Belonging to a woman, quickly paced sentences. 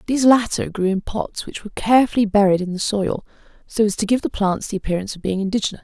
Yes: female; fast, 235 wpm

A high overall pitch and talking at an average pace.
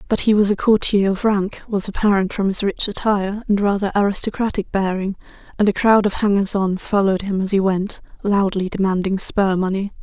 Yes: high, 200 Hz; average, 190 wpm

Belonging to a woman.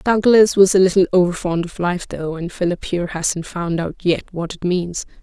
Yes: female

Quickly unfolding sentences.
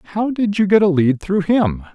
Yes: fast, 245 wpm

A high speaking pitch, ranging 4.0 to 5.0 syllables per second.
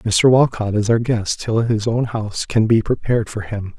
No: low, 110 Hz; 4.8 syllables/s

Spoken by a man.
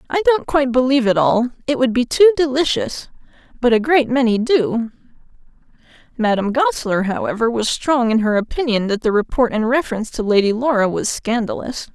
No: female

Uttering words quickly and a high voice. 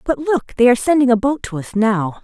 Yes: fast, 270 wpm; high, 245 Hz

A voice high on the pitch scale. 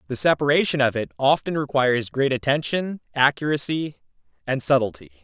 No: low, 135 Hz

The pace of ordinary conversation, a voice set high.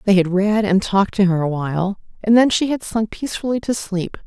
No: fast, 240 wpm; high, 200 Hz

